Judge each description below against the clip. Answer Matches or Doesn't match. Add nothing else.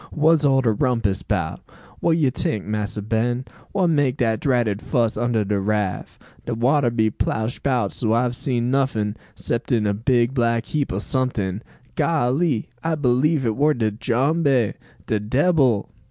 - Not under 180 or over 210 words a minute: Doesn't match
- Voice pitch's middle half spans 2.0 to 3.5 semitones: Doesn't match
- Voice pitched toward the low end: Matches